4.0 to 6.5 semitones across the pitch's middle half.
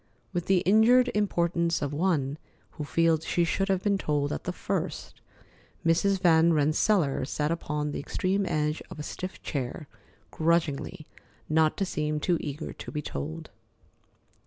No: average, 3.6 semitones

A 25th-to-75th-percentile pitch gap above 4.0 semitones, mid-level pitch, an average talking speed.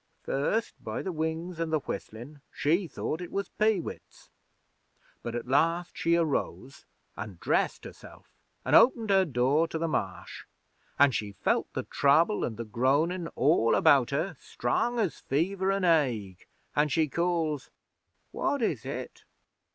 Yes: average, 5.0 semitones; medium, 160 Hz; average, 145 wpm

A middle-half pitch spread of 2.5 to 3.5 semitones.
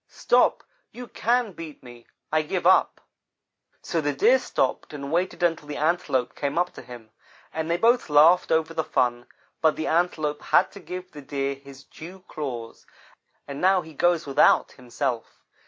No: average, 4.3 semitones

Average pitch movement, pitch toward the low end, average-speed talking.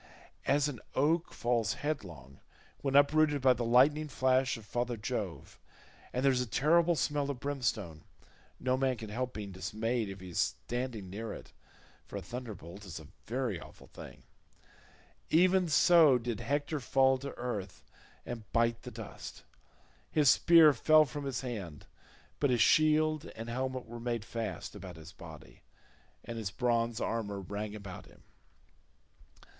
Yes: average, 4.7 semitones; low, 125 Hz; average, 150 wpm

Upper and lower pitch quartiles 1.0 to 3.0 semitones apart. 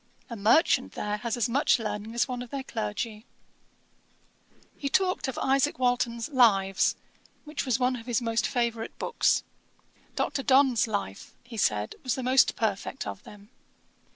No: average, 3.4 semitones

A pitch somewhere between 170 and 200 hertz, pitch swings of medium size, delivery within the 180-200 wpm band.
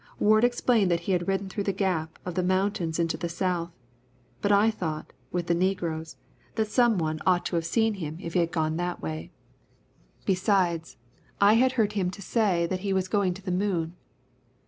Yes: medium, 185 Hz; average, 3.1 semitones; average, 190 wpm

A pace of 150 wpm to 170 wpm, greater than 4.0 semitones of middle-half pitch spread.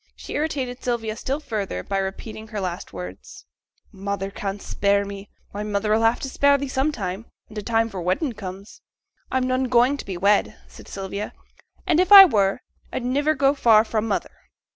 No: average, 185 wpm; average, 4.7 semitones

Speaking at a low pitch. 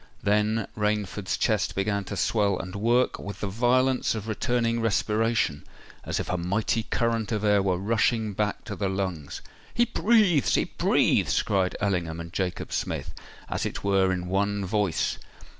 Yes: low, 105 Hz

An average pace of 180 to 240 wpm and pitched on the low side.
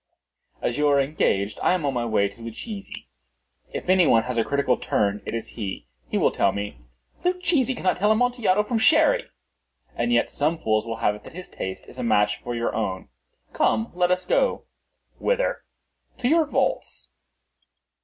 No: average, 185 wpm; medium, 145 Hz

